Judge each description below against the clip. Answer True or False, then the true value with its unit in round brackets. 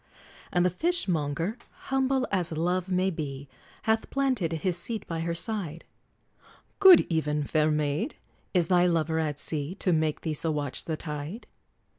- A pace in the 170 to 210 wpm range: False (155 wpm)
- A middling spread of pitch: True (3.9 semitones)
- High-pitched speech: False (170 Hz)